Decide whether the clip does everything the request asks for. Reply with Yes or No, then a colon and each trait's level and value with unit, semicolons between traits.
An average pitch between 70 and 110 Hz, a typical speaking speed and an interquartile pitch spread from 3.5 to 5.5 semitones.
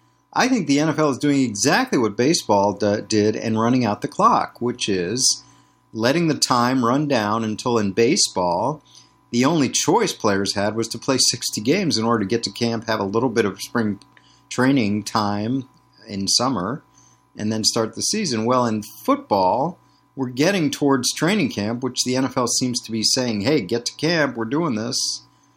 No: low, 120 Hz; average, 185 wpm; average, 4.0 semitones